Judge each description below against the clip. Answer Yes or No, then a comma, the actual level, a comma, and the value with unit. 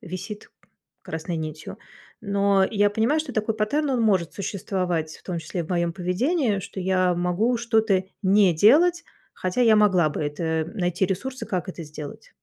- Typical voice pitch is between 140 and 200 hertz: Yes, high, 190 Hz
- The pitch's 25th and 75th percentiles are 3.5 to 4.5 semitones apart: Yes, average, 4.1 semitones